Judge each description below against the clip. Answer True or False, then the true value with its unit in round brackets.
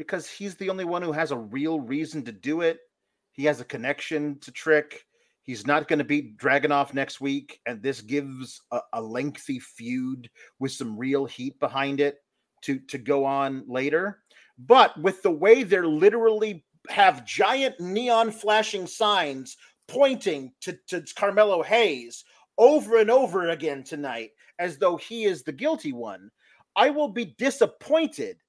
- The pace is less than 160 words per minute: False (165 wpm)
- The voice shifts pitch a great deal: True (8.1 semitones)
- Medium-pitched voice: True (160 Hz)